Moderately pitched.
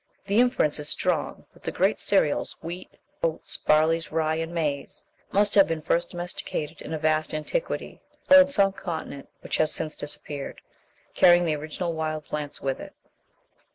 Yes: medium, 160 Hz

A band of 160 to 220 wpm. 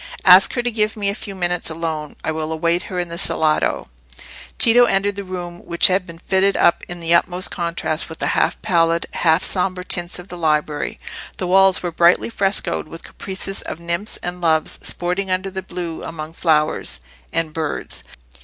Yes: average, 190 wpm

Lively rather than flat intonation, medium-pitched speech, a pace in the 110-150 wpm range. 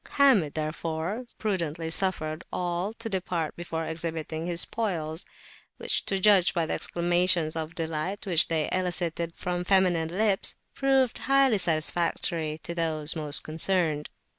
No: average, 2.9 semitones; medium, 170 Hz; slow, 135 wpm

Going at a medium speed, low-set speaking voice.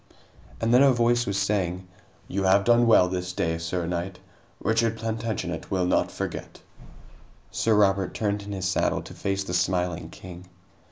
Yes: average, 165 wpm; very low, 95 Hz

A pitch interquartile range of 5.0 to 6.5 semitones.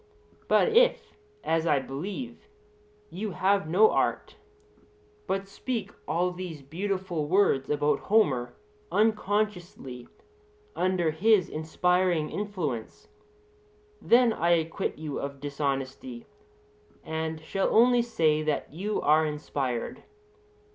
Yes: wide, 5.4 semitones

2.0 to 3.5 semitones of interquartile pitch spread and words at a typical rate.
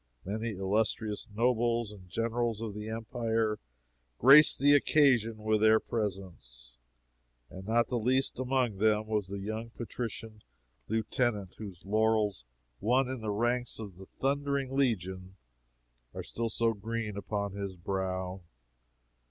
No: average, 2.9 semitones; slow, 130 wpm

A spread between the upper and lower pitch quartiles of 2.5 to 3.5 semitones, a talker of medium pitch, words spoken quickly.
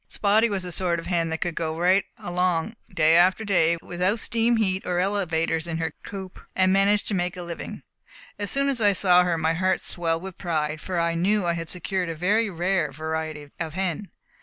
Yes: average, 2.9 semitones; medium, 180 Hz; fast, 210 wpm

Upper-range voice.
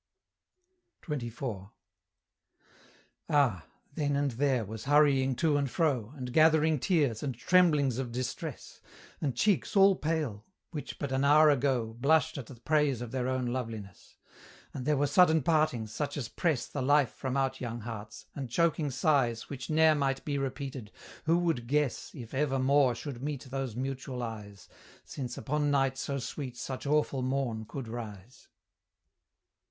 No: low, 135 Hz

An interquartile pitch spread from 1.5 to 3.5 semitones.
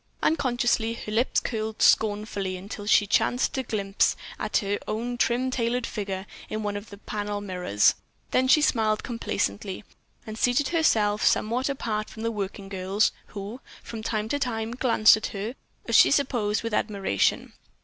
Yes: average, 2.8 semitones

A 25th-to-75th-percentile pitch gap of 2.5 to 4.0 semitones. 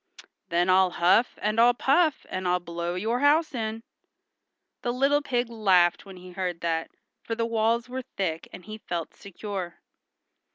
No: average, 5.1 semitones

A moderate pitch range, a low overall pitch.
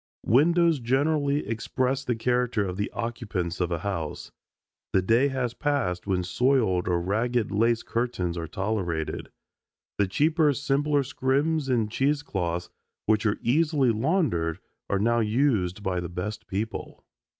No: wide, 6.5 semitones; low, 115 Hz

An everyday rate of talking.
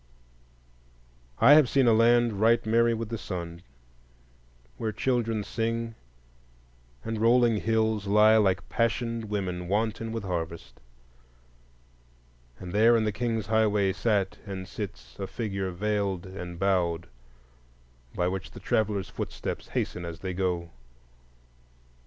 No: slow, 125 wpm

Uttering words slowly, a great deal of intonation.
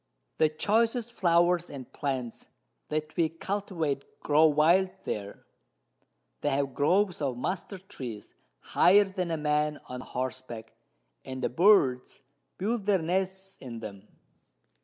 Yes: slow, 125 wpm; wide, 6.4 semitones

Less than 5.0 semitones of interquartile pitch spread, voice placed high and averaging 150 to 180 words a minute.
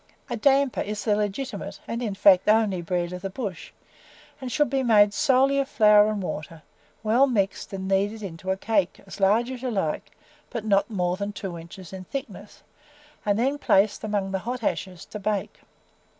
No: average, 3.4 semitones; high, 205 Hz; average, 190 wpm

